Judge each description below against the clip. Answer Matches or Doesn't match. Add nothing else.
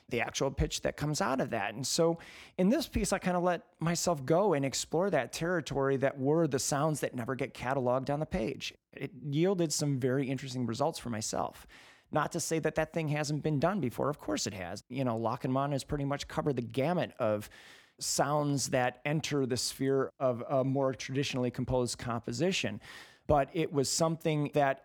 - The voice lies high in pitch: Doesn't match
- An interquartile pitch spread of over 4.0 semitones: Doesn't match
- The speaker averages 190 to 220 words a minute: Matches